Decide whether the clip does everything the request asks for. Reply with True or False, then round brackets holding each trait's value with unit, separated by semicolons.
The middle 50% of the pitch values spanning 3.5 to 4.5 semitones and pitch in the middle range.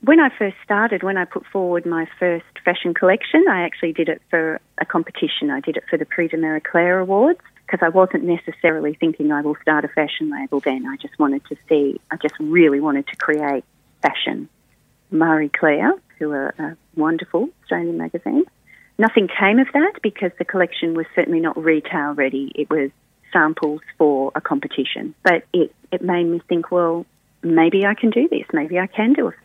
True (4.0 semitones; 170 Hz)